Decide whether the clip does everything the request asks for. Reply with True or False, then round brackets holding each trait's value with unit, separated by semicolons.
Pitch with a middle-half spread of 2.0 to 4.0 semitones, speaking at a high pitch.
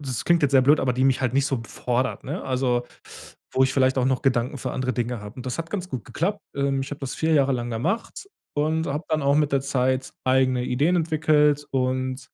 False (2.6 semitones; 135 Hz)